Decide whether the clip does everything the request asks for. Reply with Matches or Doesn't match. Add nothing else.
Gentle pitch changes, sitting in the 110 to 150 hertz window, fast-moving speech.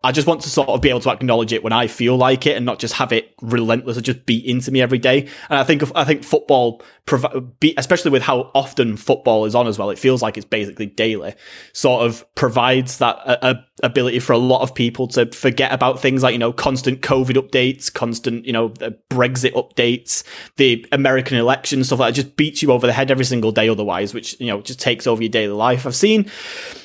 Matches